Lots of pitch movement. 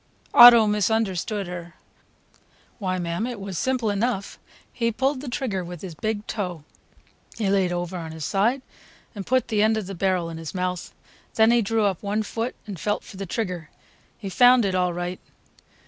No: average, 3.9 semitones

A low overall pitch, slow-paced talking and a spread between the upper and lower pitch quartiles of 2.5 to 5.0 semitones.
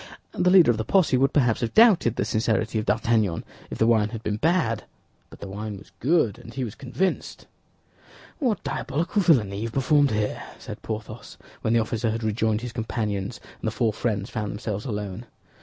No: low, 115 Hz; average, 195 wpm; average, 3.7 semitones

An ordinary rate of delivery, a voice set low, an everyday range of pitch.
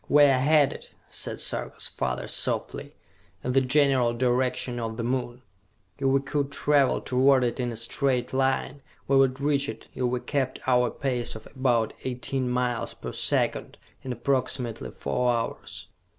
No: average, 160 wpm; low, 130 Hz; narrow, 1.9 semitones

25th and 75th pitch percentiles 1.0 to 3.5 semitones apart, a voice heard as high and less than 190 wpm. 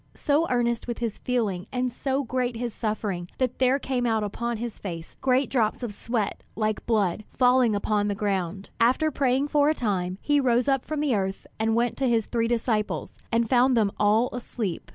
No: average, 3.2 semitones; high, 235 Hz; average, 195 wpm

